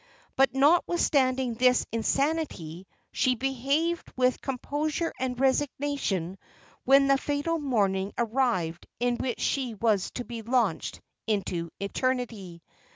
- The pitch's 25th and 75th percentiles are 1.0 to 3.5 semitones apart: No, average, 4.2 semitones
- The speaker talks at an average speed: No, slow, 110 wpm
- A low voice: No, very high, 255 Hz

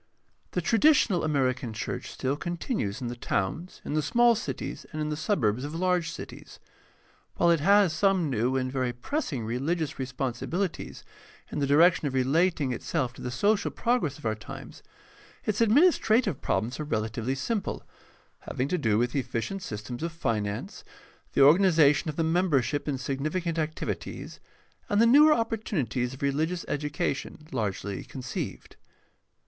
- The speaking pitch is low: No, medium, 150 Hz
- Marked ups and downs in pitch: Yes, wide, 6.2 semitones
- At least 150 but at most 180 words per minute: Yes, average, 155 wpm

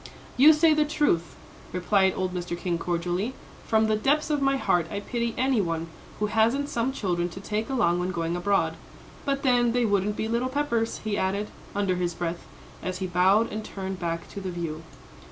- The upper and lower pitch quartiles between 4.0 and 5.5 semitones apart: Yes, average, 5.2 semitones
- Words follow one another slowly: No, average, 195 wpm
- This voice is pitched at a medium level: No, high, 205 Hz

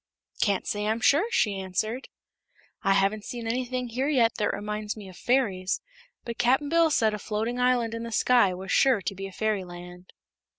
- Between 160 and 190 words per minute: Yes, average, 185 wpm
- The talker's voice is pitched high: Yes, high, 220 Hz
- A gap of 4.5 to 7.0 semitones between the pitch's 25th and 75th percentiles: No, average, 4.0 semitones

